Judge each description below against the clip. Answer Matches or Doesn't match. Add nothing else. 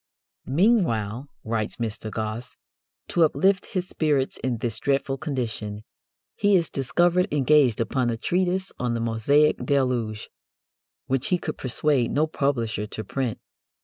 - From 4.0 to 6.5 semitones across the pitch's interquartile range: Matches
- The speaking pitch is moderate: Doesn't match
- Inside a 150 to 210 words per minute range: Doesn't match